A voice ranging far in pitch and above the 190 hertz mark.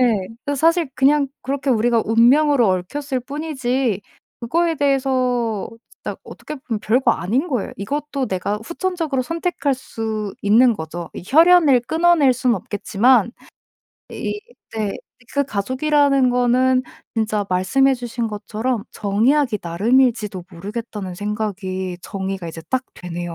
No: average, 5.0 semitones; high, 245 Hz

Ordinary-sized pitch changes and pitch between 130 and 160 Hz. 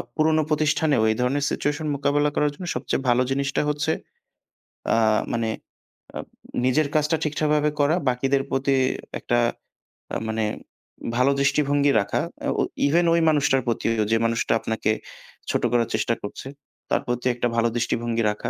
Yes: average, 4.0 semitones; medium, 140 Hz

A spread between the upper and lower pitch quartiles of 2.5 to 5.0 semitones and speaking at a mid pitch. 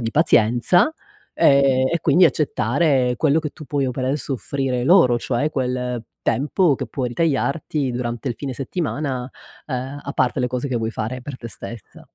No: average, 2.8 semitones; low, 130 Hz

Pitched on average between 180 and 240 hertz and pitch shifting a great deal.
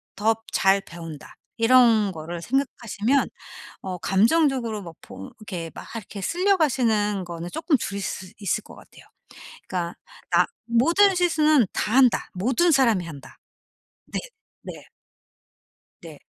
Yes: high, 220 Hz; wide, 6.4 semitones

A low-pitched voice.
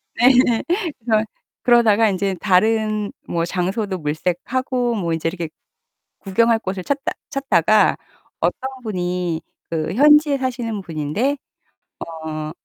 No: high, 210 Hz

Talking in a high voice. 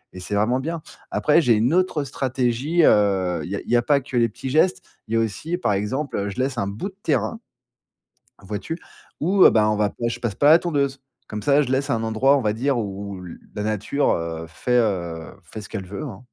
No: low, 115 Hz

